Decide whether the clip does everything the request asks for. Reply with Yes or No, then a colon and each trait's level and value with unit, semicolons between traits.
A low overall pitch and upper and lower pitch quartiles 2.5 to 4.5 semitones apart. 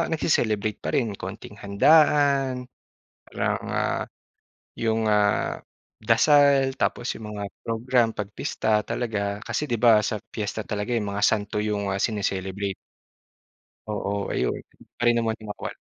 Yes: low, 110 Hz; average, 2.8 semitones